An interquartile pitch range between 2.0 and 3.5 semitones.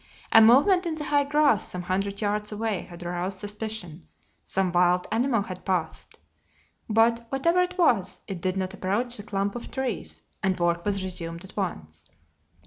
No: average, 4.4 semitones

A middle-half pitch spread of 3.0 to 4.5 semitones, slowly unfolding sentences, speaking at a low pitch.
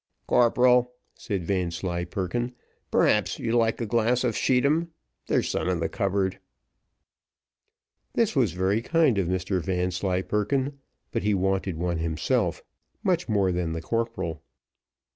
No: average, 5.1 semitones; slow, 125 wpm; low, 100 Hz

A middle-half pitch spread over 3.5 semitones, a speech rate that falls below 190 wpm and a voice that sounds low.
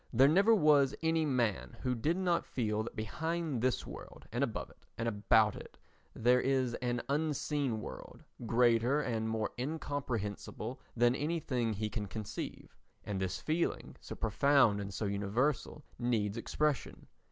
Yes: average, 5.1 semitones; average, 150 wpm; low, 125 Hz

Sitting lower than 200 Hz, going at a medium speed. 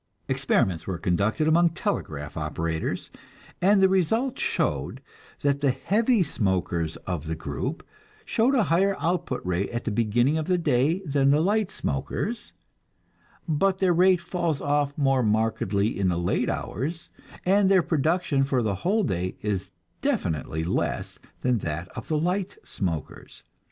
Yes: medium, 140 Hz; average, 150 wpm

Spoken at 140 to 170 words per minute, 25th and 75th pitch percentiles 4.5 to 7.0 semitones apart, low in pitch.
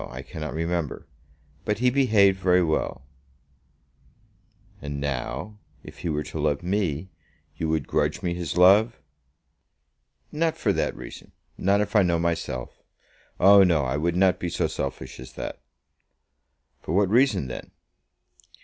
Yes: average, 145 wpm; average, 4.9 semitones; very low, 85 Hz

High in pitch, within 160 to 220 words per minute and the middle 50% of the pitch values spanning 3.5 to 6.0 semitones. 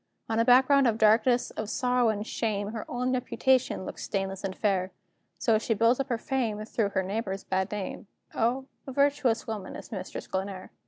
Yes: high, 225 Hz; average, 190 wpm; average, 3.8 semitones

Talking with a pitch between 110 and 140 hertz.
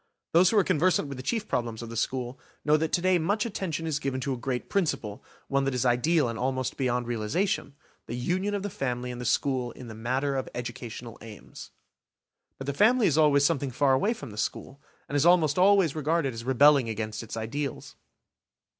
Yes: low, 135 Hz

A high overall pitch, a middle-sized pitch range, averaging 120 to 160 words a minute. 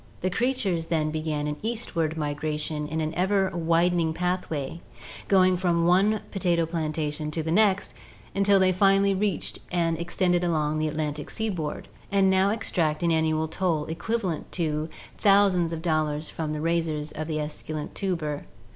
No: medium, 165 Hz; average, 3.3 semitones; average, 155 wpm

